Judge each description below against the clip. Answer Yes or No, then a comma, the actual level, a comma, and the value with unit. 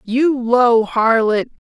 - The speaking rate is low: Yes, slow, 105 wpm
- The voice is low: No, high, 235 Hz